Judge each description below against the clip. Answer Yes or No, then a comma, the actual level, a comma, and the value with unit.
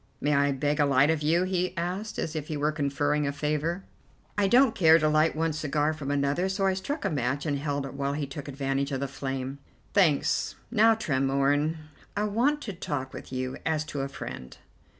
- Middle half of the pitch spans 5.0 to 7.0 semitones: No, average, 3.5 semitones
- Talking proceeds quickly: Yes, fast, 210 wpm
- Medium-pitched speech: Yes, medium, 150 Hz